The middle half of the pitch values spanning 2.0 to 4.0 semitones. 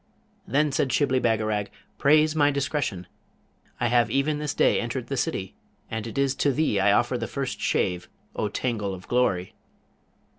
No: average, 4.9 semitones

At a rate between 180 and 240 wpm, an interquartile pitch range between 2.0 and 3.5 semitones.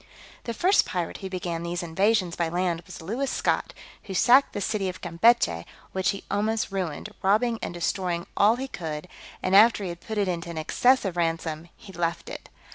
No: average, 195 wpm; average, 4.0 semitones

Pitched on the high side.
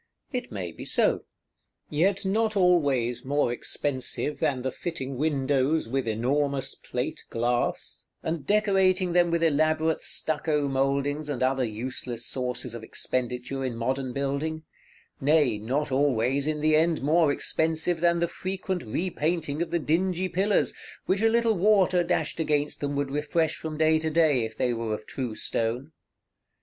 No: medium, 150 Hz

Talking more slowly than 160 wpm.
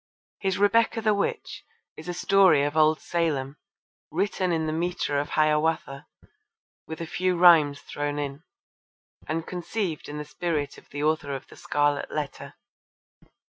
Yes: average, 150 wpm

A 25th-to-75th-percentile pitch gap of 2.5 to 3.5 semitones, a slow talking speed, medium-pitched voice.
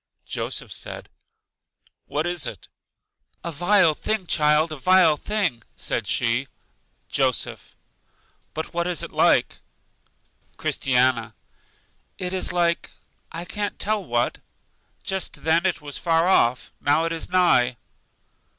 No: average, 4.3 semitones; slow, 125 wpm; medium, 165 Hz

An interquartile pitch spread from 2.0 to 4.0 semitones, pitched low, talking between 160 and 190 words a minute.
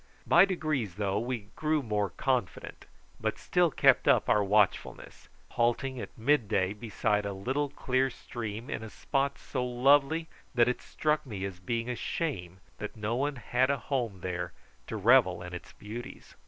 No: average, 4.9 semitones; low, 120 Hz; average, 170 wpm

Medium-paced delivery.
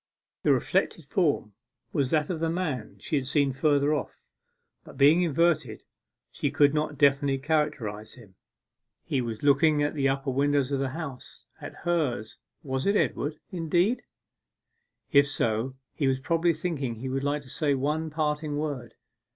Yes: average, 160 wpm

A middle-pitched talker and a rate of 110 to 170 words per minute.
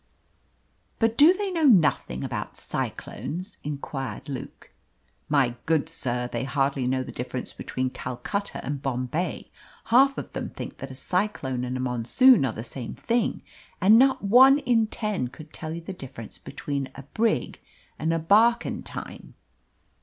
Yes: medium, 155 Hz; average, 155 wpm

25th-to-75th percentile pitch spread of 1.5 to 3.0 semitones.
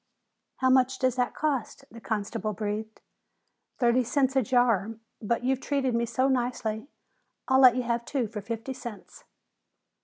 Yes: average, 2.7 semitones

